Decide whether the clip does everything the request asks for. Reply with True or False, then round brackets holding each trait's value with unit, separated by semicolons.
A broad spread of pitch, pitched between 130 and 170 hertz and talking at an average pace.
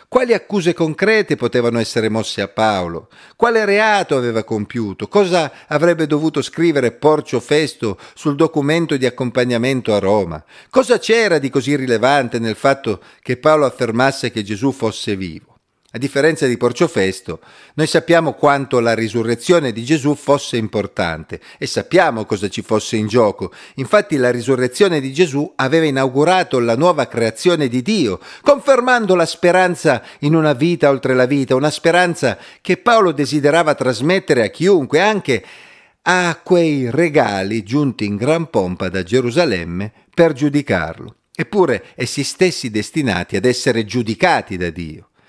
True (6.4 semitones; 140 Hz; 145 wpm)